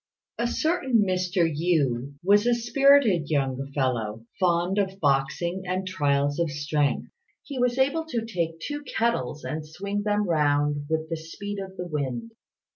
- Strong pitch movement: Yes, wide, 6.1 semitones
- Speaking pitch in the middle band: Yes, medium, 175 Hz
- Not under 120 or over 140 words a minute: No, average, 160 wpm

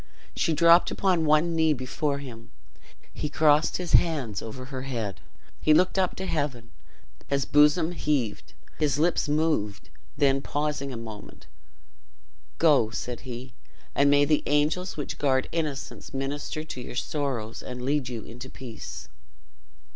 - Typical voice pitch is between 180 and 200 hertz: No, medium, 145 Hz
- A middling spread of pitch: Yes, average, 3.6 semitones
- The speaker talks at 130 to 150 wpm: Yes, average, 145 wpm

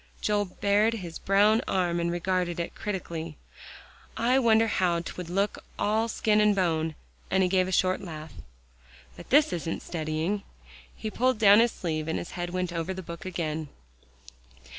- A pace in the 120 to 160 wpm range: No, average, 170 wpm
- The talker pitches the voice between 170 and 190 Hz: Yes, medium, 185 Hz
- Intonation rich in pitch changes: No, average, 3.7 semitones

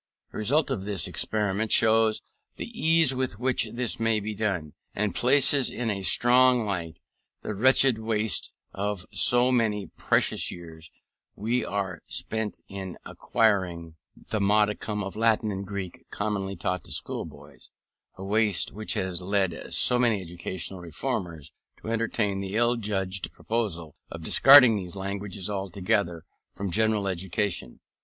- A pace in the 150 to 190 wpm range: No, average, 140 wpm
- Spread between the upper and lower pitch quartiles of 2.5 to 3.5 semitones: Yes, average, 3.1 semitones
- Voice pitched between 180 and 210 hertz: No, low, 105 Hz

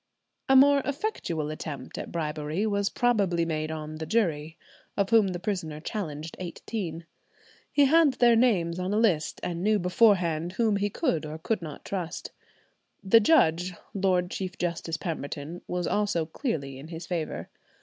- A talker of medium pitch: Yes, medium, 180 Hz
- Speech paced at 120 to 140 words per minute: No, average, 160 wpm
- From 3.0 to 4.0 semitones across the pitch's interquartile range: No, average, 4.9 semitones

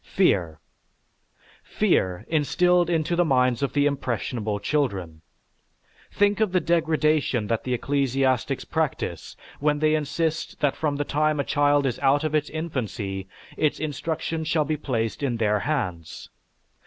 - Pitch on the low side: No, medium, 145 Hz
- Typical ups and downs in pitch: Yes, average, 4.8 semitones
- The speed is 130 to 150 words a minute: Yes, average, 140 wpm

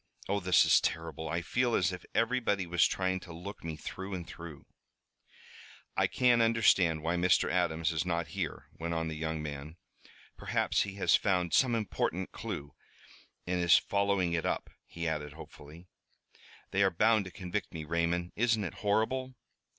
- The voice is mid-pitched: No, very low, 90 Hz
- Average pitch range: Yes, average, 3.6 semitones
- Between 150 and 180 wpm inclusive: Yes, average, 170 wpm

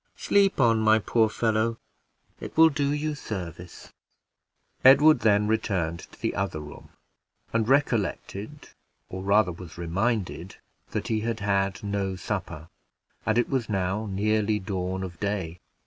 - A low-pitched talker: Yes, low, 105 Hz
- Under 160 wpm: Yes, average, 140 wpm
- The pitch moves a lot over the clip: No, average, 3.5 semitones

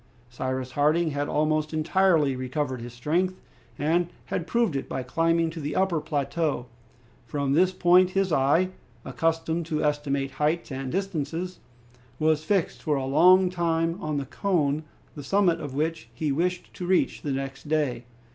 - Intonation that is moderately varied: Yes, average, 3.6 semitones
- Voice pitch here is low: No, medium, 155 Hz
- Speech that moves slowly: No, average, 160 wpm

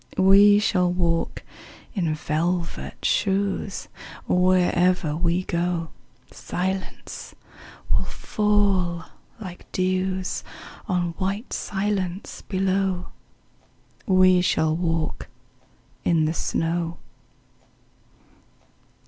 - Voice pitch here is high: No, medium, 180 Hz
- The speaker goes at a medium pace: No, slow, 75 wpm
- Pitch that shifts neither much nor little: No, narrow, 2.0 semitones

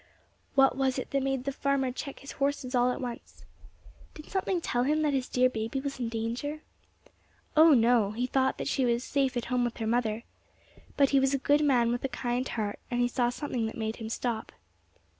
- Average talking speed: No, fast, 215 wpm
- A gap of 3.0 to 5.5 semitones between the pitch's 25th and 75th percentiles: No, narrow, 2.6 semitones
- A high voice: Yes, very high, 255 Hz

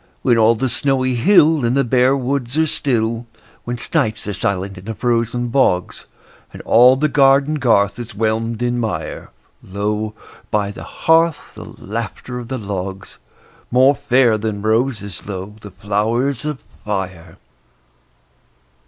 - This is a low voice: Yes, low, 115 Hz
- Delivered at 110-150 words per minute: Yes, average, 145 wpm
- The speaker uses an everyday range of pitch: Yes, average, 4.0 semitones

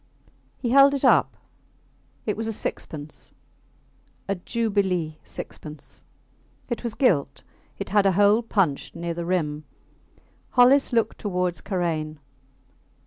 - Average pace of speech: No, slow, 120 wpm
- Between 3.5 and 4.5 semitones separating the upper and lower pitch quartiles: No, wide, 5.4 semitones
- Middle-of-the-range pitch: No, high, 195 Hz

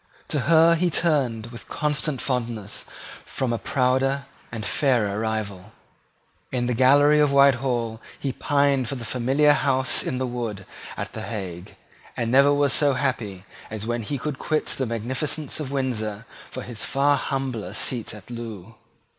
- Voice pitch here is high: No, low, 125 Hz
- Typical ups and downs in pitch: Yes, average, 3.8 semitones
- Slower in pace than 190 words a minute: Yes, average, 160 wpm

